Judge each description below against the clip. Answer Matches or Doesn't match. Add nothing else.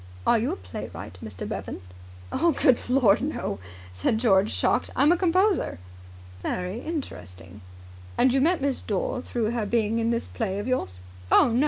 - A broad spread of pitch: Matches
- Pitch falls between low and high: Doesn't match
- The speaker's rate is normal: Matches